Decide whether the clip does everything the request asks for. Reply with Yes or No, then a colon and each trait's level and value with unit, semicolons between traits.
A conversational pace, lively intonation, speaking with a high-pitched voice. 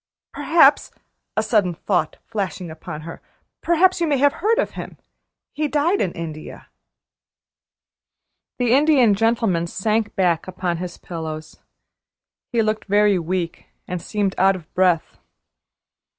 No: slow, 130 wpm; wide, 6.2 semitones; high, 195 Hz